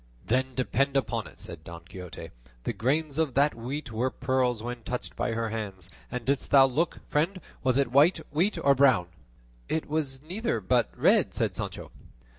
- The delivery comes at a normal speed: Yes, average, 180 wpm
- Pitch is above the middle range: No, low, 130 Hz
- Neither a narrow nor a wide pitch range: Yes, average, 3.8 semitones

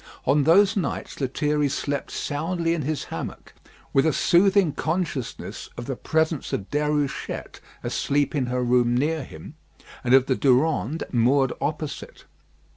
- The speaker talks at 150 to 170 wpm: No, average, 140 wpm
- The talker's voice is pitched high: No, medium, 145 Hz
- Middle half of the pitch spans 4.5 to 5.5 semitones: No, average, 3.4 semitones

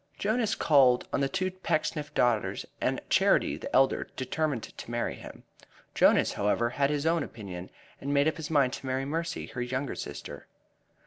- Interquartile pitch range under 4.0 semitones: No, average, 4.3 semitones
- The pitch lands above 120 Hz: Yes, medium, 140 Hz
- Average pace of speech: Yes, average, 175 wpm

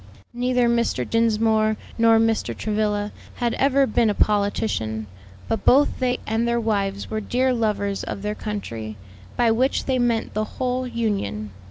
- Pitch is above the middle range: Yes, high, 225 Hz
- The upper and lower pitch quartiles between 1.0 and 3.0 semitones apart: Yes, average, 2.7 semitones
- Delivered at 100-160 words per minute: Yes, average, 155 wpm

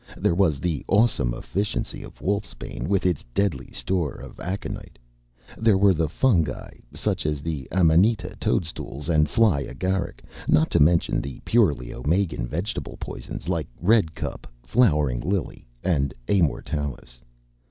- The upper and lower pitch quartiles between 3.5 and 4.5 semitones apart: No, average, 5.1 semitones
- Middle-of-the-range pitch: No, very low, 85 Hz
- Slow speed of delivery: Yes, slow, 130 wpm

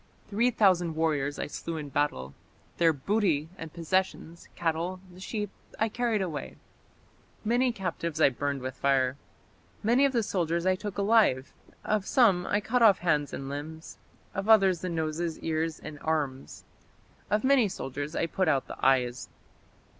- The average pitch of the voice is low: No, medium, 170 Hz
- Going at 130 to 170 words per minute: Yes, average, 155 wpm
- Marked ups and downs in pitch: Yes, wide, 5.7 semitones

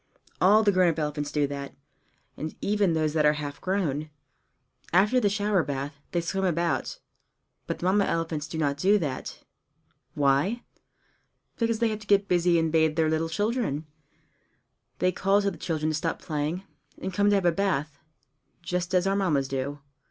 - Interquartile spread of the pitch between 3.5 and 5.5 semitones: Yes, average, 4.6 semitones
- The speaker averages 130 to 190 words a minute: Yes, average, 180 wpm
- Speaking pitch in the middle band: Yes, medium, 170 Hz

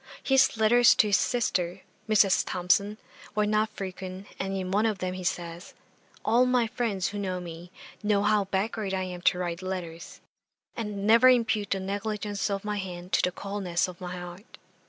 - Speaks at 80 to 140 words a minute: No, average, 180 wpm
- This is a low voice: No, high, 195 Hz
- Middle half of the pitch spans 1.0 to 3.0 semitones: Yes, average, 2.7 semitones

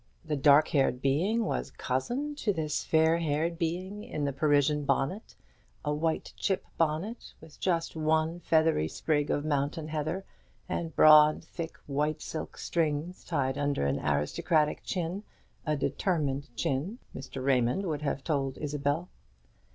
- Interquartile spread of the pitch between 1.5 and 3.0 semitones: Yes, average, 2.7 semitones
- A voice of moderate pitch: Yes, medium, 155 Hz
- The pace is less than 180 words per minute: Yes, average, 145 wpm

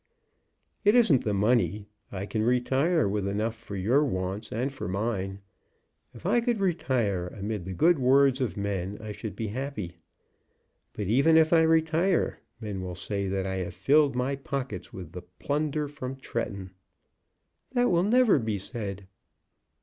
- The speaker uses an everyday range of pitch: No, wide, 6.6 semitones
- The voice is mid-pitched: No, low, 115 Hz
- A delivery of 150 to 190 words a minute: Yes, average, 155 wpm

